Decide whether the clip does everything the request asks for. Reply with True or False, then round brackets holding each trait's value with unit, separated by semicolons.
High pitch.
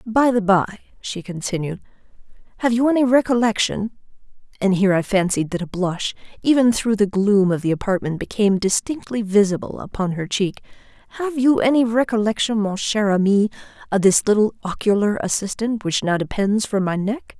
True (210 Hz)